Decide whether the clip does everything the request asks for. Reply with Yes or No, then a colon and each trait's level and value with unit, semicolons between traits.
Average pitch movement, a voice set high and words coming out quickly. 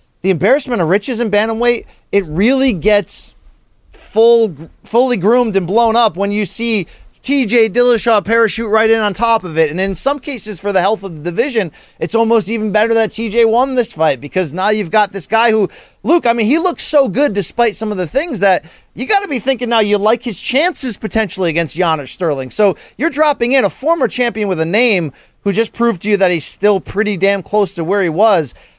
Yes: average, 3.2 semitones; high, 220 Hz; fast, 215 wpm